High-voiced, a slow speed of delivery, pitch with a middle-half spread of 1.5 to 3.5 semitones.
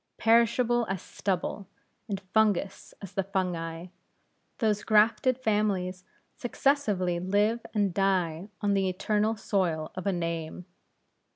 Yes: high, 195 Hz; slow, 115 wpm; average, 3.1 semitones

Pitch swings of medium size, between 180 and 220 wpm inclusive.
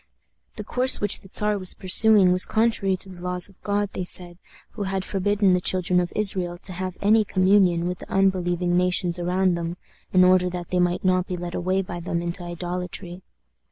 No: narrow, 1.6 semitones; average, 200 wpm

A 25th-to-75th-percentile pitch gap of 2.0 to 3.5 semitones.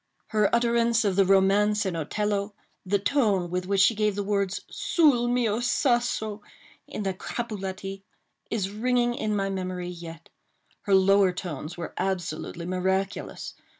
Yes: narrow, 2.6 semitones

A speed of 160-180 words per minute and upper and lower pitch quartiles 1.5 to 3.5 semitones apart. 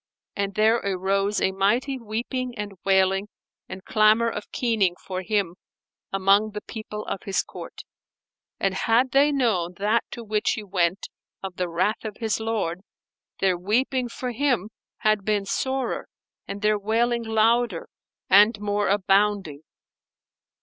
No: average, 145 wpm; average, 2.9 semitones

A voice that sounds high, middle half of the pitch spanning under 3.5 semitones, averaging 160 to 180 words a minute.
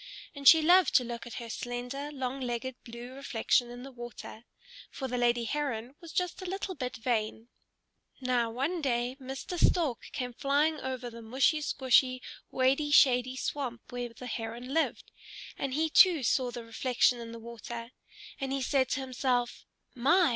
Yes: very high, 255 Hz; narrow, 2.6 semitones; average, 170 wpm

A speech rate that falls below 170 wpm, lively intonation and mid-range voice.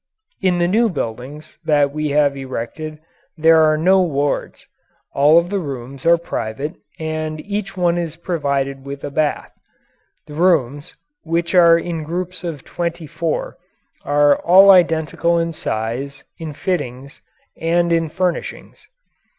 No: average, 140 wpm; average, 3.2 semitones; medium, 155 Hz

